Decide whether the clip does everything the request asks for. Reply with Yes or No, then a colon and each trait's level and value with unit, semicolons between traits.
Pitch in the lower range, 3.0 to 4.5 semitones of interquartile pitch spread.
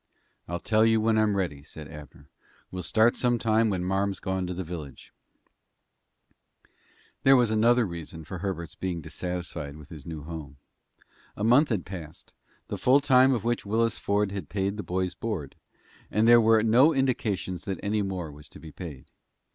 No: very low, 95 Hz; average, 5.1 semitones